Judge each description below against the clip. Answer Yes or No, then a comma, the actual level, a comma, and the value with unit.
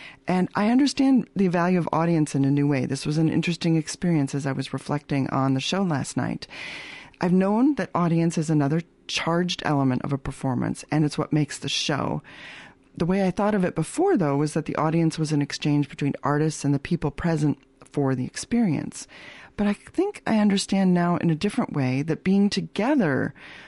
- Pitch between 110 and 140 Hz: No, medium, 160 Hz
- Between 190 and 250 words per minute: Yes, average, 200 wpm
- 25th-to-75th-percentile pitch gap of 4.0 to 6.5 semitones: Yes, average, 4.5 semitones